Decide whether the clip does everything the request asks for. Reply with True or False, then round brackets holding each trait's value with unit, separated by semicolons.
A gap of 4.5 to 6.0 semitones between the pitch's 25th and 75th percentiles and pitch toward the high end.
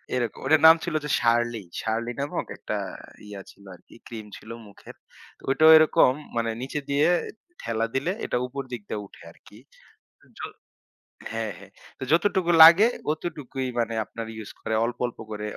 False (5.1 semitones; 120 Hz)